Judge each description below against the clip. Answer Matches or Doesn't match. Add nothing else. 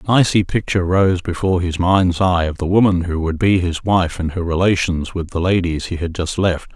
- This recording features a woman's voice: Doesn't match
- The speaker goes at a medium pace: Doesn't match